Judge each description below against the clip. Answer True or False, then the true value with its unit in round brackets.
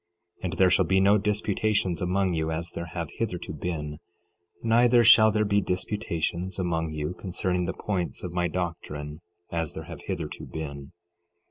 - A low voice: True (90 Hz)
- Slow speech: False (160 wpm)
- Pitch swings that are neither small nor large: True (3.3 semitones)